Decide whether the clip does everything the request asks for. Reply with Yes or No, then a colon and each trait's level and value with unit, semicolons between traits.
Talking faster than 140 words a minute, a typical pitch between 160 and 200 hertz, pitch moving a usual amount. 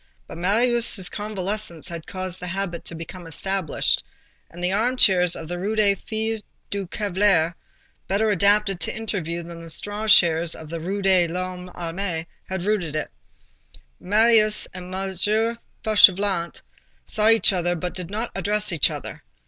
Yes: average, 155 wpm; high, 190 Hz; average, 3.3 semitones